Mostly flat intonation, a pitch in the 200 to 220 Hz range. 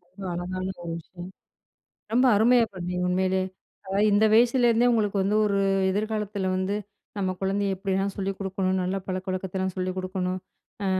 No: narrow, 1.8 semitones; high, 190 Hz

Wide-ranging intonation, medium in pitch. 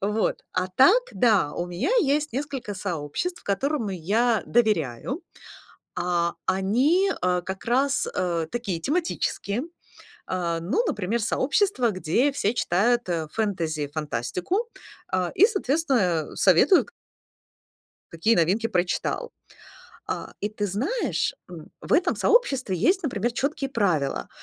No: wide, 7.5 semitones; high, 210 Hz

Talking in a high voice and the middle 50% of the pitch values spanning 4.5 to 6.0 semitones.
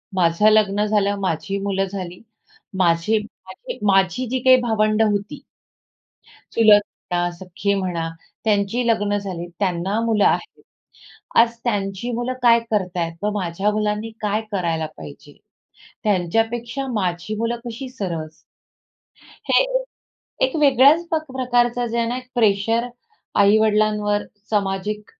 No: high, 210 Hz; average, 3.6 semitones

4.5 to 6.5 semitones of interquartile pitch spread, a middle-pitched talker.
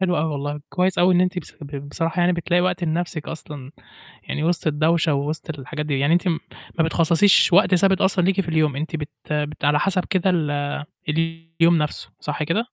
No: average, 3.0 semitones; medium, 165 Hz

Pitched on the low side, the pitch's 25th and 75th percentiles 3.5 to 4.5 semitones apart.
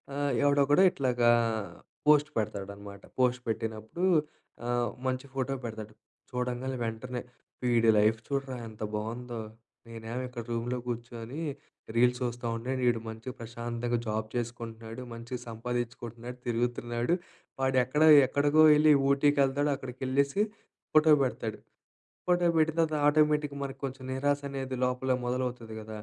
No: low, 125 Hz; average, 3.0 semitones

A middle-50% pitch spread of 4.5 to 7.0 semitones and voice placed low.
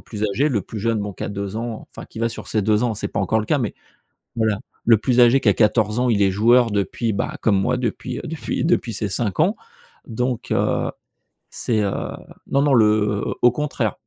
No: average, 2.9 semitones; low, 110 Hz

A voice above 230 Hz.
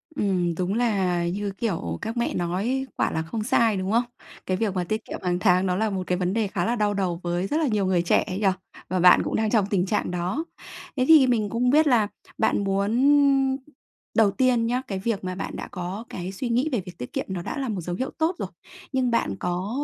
No: high, 200 Hz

